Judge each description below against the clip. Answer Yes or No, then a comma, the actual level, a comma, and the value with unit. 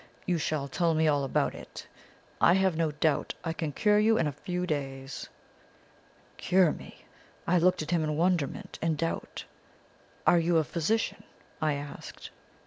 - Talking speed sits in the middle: Yes, average, 165 wpm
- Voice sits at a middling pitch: Yes, medium, 160 Hz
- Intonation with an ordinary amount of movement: Yes, average, 3.1 semitones